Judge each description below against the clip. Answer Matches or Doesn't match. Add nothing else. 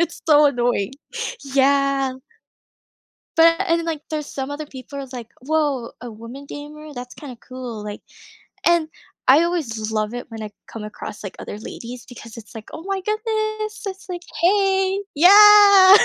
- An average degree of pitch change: Doesn't match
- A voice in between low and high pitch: Doesn't match